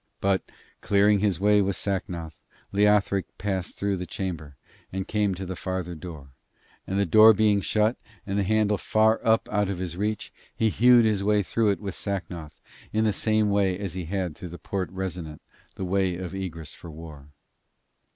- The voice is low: Yes, very low, 95 Hz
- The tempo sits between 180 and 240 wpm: Yes, average, 185 wpm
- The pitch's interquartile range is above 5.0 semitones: No, average, 2.7 semitones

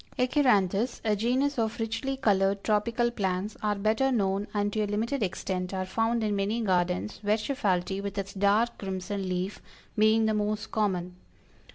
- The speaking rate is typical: Yes, average, 160 wpm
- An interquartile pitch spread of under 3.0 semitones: Yes, narrow, 2.6 semitones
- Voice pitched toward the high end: Yes, high, 210 Hz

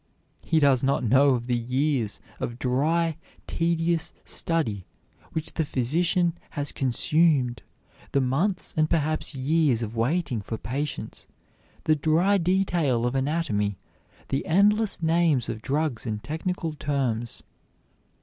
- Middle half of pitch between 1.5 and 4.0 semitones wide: No, average, 5.0 semitones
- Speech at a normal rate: No, slow, 125 wpm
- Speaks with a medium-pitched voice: Yes, medium, 145 Hz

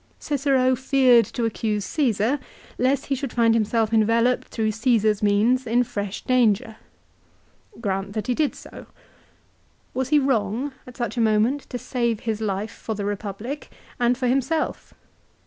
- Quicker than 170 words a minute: No, average, 150 wpm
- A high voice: Yes, high, 235 Hz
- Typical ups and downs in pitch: Yes, average, 3.1 semitones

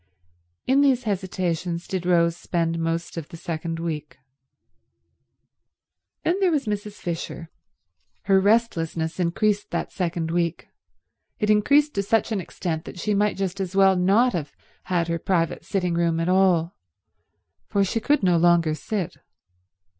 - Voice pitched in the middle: Yes, medium, 180 Hz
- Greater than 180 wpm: No, average, 145 wpm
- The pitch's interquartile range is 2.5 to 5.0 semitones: Yes, average, 3.5 semitones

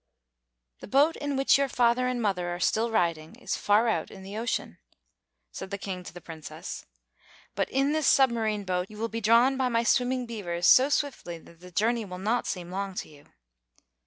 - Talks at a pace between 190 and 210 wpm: Yes, average, 200 wpm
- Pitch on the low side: No, high, 220 Hz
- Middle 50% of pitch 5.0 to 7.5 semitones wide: Yes, wide, 5.4 semitones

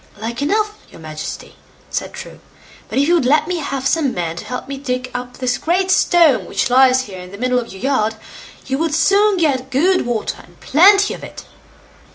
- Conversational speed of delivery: No, fast, 210 wpm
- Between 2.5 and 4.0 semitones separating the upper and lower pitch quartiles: No, average, 5.1 semitones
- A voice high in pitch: Yes, very high, 270 Hz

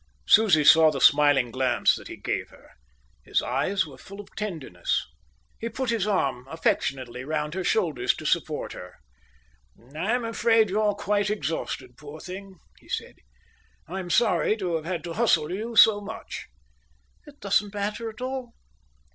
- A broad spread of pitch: Yes, wide, 6.1 semitones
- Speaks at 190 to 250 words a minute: No, average, 155 wpm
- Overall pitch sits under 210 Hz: Yes, high, 190 Hz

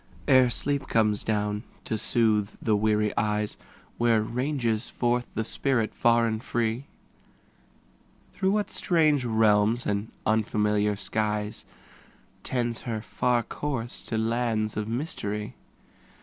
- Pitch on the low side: Yes, low, 110 Hz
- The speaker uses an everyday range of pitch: No, narrow, 2.3 semitones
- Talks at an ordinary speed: No, slow, 120 wpm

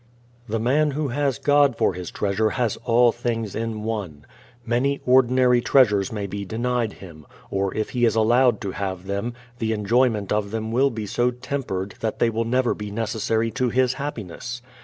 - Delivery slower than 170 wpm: No, average, 180 wpm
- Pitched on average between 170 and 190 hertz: No, low, 115 Hz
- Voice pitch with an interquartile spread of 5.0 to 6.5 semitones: No, average, 3.2 semitones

